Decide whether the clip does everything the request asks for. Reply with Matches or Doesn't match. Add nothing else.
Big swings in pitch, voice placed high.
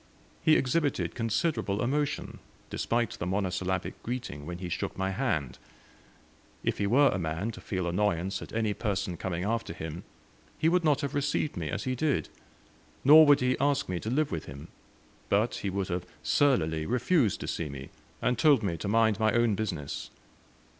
Doesn't match